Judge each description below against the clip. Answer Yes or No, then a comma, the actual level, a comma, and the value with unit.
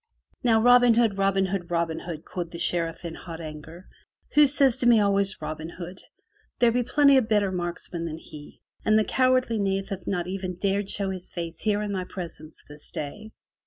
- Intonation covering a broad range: No, average, 4.3 semitones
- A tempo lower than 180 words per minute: No, average, 200 wpm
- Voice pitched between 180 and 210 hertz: Yes, high, 190 Hz